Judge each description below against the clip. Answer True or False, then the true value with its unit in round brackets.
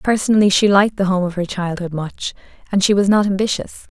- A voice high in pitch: True (195 Hz)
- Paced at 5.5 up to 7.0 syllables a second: True (6.0 syllables/s)